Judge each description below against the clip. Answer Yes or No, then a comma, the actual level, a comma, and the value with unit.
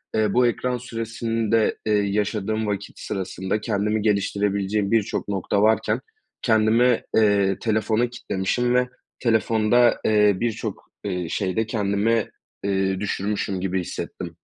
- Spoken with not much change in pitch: Yes, narrow, 2.2 semitones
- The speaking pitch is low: Yes, low, 105 Hz